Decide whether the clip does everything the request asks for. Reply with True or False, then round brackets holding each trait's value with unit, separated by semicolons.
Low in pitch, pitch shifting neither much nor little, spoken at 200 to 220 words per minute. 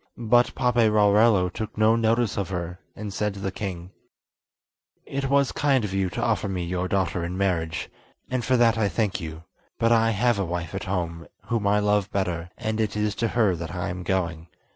True (100 Hz; 3.9 semitones; 205 wpm)